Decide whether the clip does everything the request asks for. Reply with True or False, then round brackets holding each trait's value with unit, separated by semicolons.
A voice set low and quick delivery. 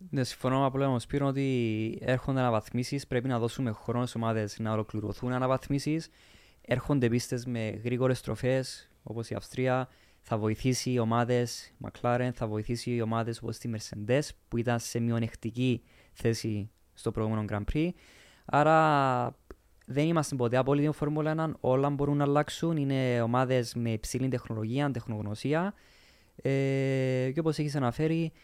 False (125 Hz; 150 wpm)